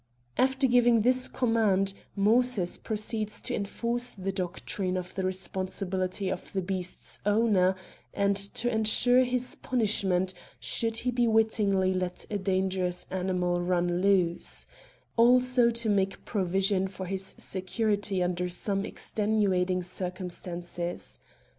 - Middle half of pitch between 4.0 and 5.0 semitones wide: No, average, 3.2 semitones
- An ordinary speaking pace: No, slow, 115 wpm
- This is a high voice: Yes, high, 195 Hz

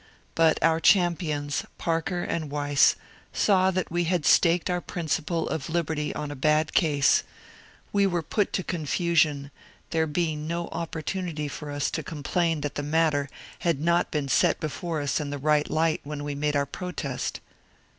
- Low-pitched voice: No, medium, 160 Hz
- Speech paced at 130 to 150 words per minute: No, average, 170 wpm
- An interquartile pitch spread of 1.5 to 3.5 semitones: Yes, average, 2.8 semitones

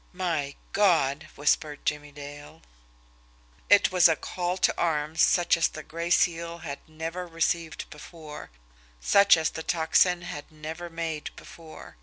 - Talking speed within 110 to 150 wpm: Yes, average, 140 wpm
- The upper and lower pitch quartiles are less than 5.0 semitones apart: Yes, narrow, 2.5 semitones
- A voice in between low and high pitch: Yes, medium, 160 Hz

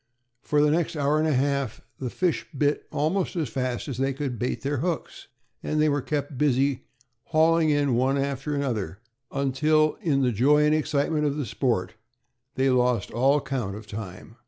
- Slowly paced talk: No, average, 180 wpm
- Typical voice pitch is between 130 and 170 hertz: Yes, medium, 140 Hz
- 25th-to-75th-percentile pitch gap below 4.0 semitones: Yes, average, 3.0 semitones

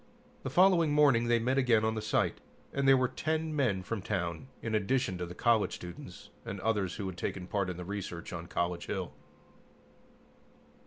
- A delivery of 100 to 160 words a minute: No, average, 190 wpm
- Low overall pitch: Yes, low, 110 Hz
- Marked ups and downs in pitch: Yes, wide, 6.0 semitones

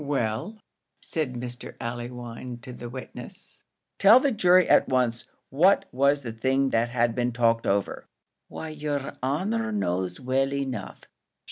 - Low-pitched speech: Yes, low, 130 Hz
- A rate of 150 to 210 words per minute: No, average, 140 wpm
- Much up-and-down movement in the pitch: No, average, 3.7 semitones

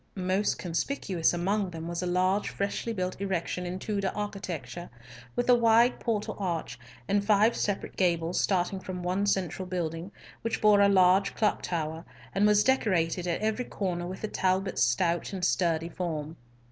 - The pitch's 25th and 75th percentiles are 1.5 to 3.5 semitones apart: Yes, average, 2.9 semitones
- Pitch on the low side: No, medium, 185 Hz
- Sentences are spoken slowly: No, average, 165 wpm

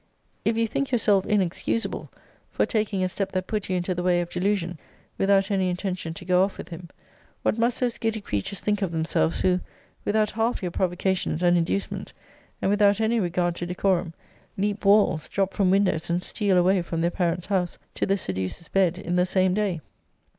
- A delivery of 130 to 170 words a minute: No, average, 195 wpm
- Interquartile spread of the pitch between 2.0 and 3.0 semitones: Yes, narrow, 2.6 semitones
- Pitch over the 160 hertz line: Yes, medium, 185 Hz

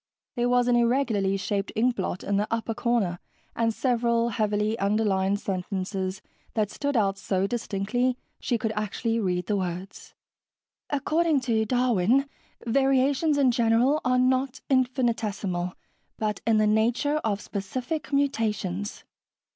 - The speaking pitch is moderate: No, high, 225 Hz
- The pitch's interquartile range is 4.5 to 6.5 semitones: No, average, 4.0 semitones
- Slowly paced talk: Yes, slow, 130 wpm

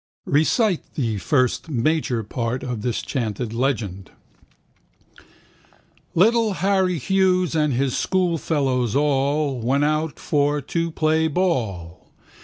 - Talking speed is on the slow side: Yes, slow, 105 wpm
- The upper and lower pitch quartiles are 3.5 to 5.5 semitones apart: Yes, average, 5.1 semitones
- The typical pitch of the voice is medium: Yes, medium, 145 Hz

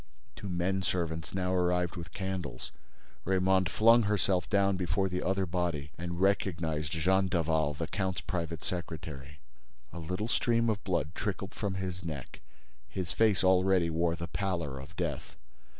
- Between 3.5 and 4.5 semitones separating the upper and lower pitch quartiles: No, narrow, 2.6 semitones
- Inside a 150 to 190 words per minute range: Yes, average, 155 wpm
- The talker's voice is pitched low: Yes, very low, 90 Hz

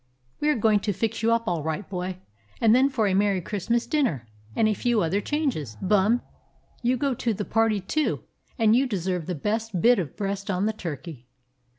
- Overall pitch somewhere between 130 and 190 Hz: No, high, 210 Hz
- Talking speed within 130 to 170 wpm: No, fast, 205 wpm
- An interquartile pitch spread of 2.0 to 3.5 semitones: No, average, 4.1 semitones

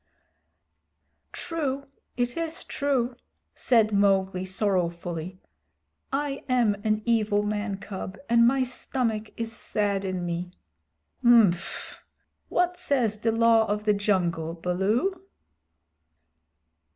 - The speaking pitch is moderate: No, high, 215 Hz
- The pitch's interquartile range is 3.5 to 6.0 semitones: Yes, average, 4.2 semitones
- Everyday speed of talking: No, slow, 105 wpm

